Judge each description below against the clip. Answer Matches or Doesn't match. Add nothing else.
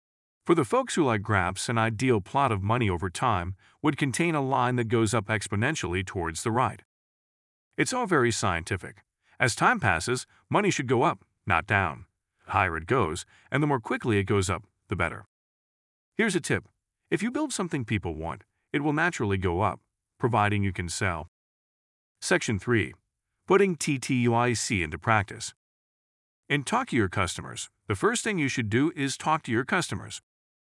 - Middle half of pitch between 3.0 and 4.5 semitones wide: Doesn't match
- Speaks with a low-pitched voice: Matches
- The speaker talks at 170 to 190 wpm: Matches